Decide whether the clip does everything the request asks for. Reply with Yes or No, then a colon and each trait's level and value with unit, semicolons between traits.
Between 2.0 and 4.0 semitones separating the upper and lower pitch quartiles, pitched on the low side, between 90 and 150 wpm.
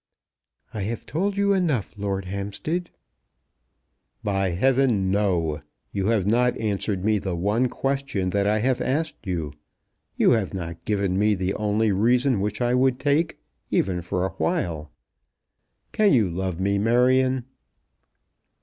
No: average, 4.9 semitones; low, 105 Hz; average, 140 wpm